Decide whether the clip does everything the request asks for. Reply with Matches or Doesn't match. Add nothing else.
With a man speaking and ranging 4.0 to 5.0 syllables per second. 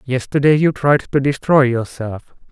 Matches